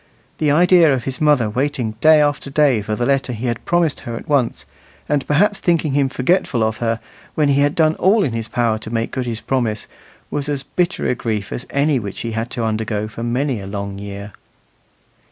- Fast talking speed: Yes, fast, 215 wpm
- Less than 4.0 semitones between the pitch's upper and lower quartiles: No, average, 4.7 semitones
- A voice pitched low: Yes, low, 130 Hz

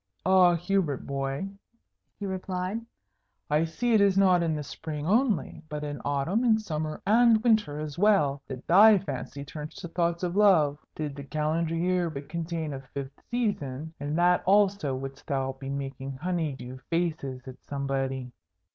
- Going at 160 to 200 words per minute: Yes, average, 165 wpm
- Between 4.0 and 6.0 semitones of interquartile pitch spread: Yes, average, 5.2 semitones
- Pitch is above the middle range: No, medium, 160 Hz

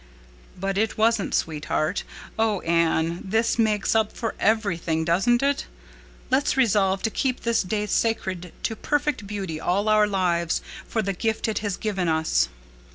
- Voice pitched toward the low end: No, high, 205 Hz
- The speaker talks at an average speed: Yes, average, 155 wpm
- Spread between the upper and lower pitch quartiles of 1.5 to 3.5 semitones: No, average, 4.1 semitones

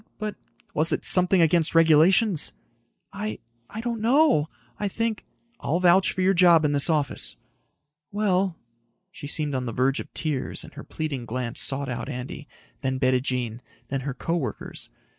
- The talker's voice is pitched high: No, medium, 155 Hz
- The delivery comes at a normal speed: Yes, average, 160 wpm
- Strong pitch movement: Yes, wide, 6.1 semitones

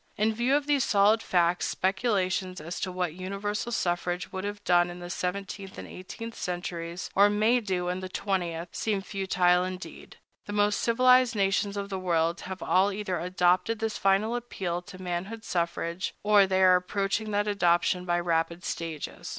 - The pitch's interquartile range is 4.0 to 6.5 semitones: No, narrow, 2.6 semitones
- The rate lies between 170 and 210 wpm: Yes, average, 175 wpm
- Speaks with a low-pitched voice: No, high, 190 Hz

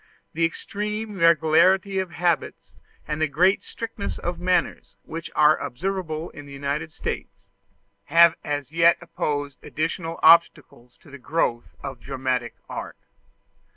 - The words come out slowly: Yes, slow, 130 wpm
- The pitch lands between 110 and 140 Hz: No, medium, 160 Hz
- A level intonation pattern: No, average, 3.6 semitones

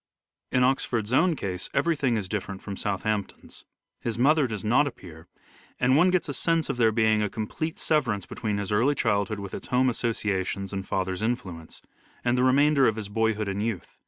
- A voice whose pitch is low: Yes, low, 110 Hz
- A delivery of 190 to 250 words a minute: Yes, average, 200 wpm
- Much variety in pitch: No, average, 4.3 semitones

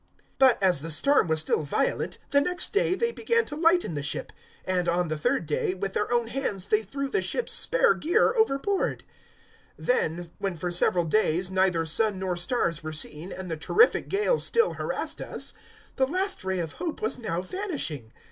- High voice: Yes, high, 195 Hz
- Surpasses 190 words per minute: Yes, average, 200 wpm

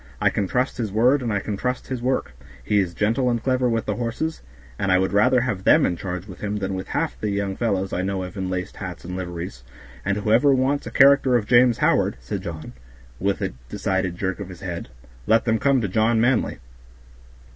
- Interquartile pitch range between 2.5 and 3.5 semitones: No, average, 4.6 semitones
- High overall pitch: No, low, 105 Hz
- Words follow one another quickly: Yes, fast, 225 wpm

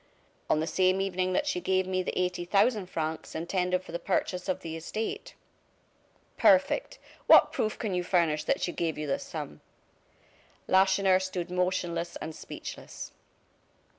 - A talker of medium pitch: Yes, medium, 180 Hz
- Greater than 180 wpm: No, average, 155 wpm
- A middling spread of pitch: No, narrow, 1.9 semitones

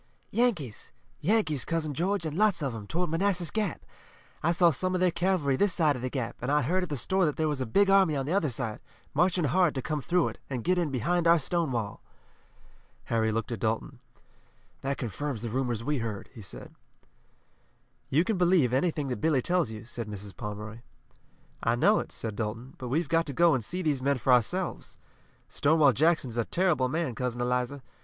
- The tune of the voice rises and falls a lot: Yes, wide, 6.0 semitones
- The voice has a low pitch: No, medium, 145 Hz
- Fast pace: Yes, fast, 210 wpm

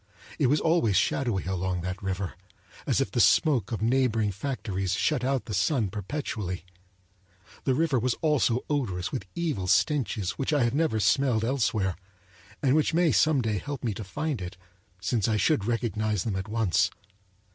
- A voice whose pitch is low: Yes, low, 115 Hz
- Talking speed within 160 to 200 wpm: Yes, average, 170 wpm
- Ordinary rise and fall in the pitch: No, wide, 6.1 semitones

